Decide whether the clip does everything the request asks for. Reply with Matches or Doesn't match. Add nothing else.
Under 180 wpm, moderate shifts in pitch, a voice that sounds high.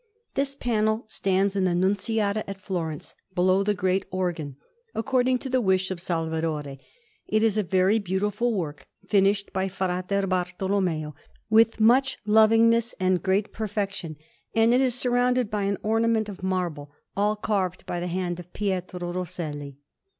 Matches